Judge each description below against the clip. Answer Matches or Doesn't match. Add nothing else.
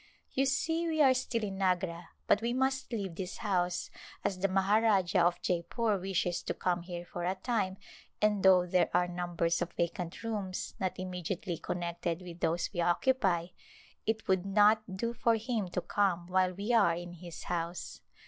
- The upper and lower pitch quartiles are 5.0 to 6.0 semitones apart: Doesn't match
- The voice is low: Doesn't match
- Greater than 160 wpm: Matches